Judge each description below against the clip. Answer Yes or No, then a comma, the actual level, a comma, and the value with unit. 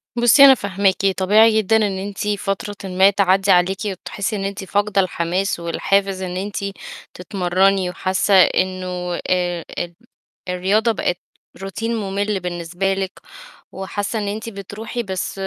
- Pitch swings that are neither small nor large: No, narrow, 1.8 semitones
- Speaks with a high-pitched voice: Yes, high, 195 Hz